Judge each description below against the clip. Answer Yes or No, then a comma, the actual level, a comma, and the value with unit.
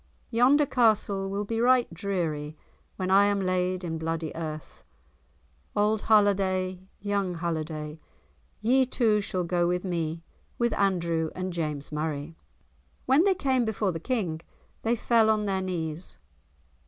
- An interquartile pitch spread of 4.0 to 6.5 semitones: Yes, average, 4.7 semitones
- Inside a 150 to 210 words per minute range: No, average, 140 wpm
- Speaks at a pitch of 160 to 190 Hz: Yes, medium, 185 Hz